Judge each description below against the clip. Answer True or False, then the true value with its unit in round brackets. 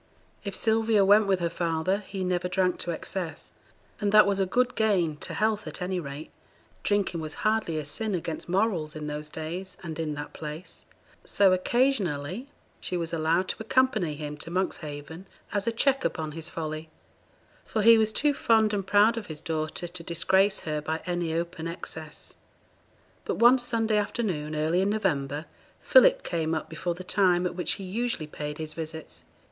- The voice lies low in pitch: False (180 Hz)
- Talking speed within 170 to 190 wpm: True (180 wpm)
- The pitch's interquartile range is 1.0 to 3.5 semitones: False (4.8 semitones)